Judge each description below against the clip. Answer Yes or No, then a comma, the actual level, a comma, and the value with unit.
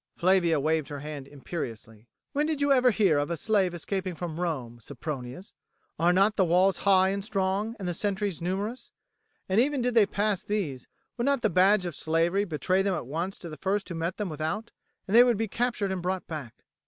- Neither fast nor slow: No, fast, 210 wpm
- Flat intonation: No, average, 4.5 semitones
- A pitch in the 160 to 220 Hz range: Yes, medium, 185 Hz